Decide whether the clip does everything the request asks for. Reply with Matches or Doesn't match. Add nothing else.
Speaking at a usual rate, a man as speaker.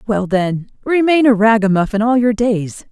Doesn't match